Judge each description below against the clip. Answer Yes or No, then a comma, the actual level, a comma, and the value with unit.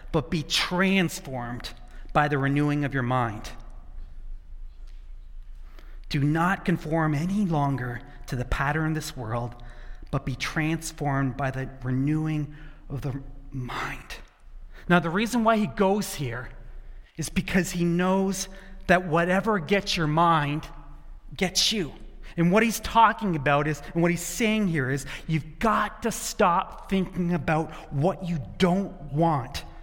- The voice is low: No, medium, 155 Hz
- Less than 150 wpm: Yes, average, 140 wpm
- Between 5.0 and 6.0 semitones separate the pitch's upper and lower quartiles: Yes, wide, 5.4 semitones